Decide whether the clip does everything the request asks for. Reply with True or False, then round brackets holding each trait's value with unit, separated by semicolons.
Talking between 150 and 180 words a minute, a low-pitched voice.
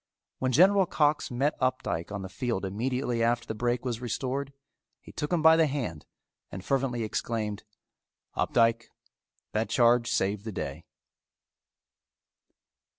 False (135 wpm; 120 Hz)